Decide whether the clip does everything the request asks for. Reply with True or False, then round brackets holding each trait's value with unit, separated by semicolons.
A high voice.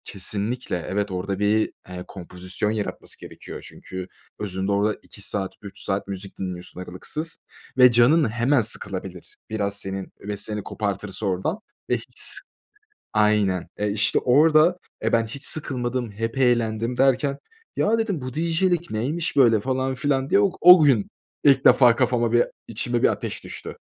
False (110 Hz)